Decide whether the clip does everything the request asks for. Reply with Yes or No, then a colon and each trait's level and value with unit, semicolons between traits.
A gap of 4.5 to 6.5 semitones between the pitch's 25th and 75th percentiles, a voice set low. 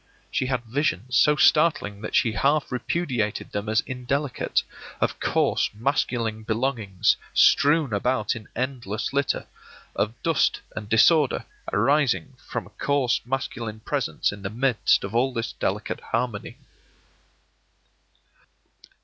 No: average, 4.0 semitones; low, 125 Hz